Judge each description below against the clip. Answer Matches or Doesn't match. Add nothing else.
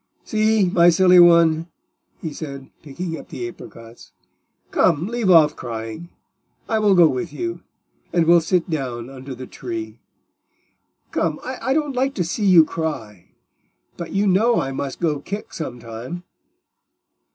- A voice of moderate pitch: Matches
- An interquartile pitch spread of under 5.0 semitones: Doesn't match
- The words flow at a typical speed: Matches